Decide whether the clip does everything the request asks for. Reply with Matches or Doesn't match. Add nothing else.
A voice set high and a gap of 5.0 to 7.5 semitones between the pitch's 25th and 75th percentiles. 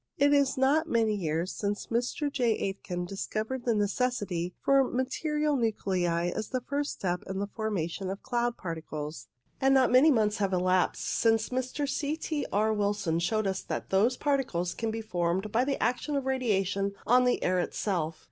Matches